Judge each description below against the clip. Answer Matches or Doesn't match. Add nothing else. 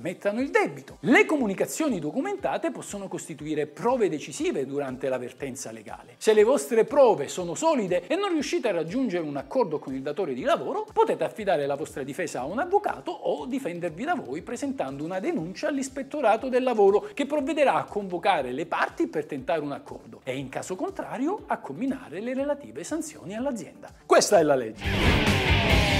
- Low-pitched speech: Doesn't match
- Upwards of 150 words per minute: Matches